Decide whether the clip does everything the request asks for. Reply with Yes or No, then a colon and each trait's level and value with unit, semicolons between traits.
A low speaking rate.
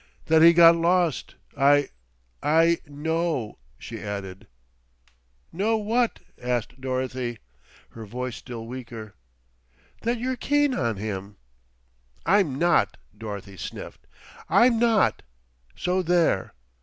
Yes: slow, 105 wpm